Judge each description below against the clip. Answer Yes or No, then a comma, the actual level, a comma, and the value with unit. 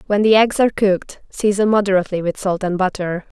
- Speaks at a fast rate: No, average, 195 wpm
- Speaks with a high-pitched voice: Yes, high, 195 Hz